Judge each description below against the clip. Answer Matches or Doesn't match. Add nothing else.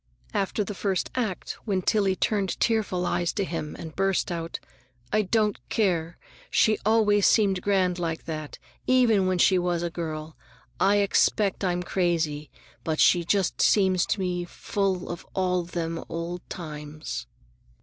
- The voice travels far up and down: Doesn't match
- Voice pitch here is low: Doesn't match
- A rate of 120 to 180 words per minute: Matches